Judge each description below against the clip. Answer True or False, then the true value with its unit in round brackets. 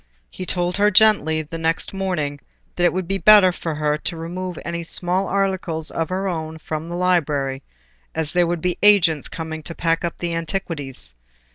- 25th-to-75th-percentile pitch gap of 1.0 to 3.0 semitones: True (2.6 semitones)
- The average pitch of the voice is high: False (170 Hz)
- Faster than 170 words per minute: True (185 wpm)